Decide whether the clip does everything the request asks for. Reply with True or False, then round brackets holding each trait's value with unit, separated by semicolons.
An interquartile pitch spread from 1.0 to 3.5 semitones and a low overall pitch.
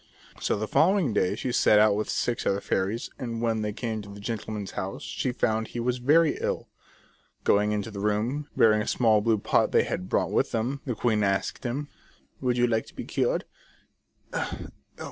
True (2.8 semitones; 110 Hz)